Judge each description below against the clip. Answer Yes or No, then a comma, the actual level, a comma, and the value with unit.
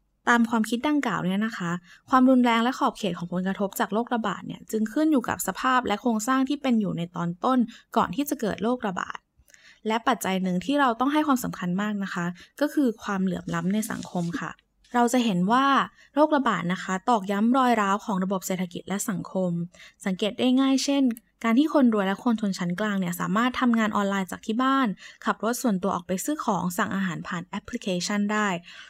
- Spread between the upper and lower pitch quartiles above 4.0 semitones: Yes, average, 4.8 semitones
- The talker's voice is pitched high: Yes, high, 220 Hz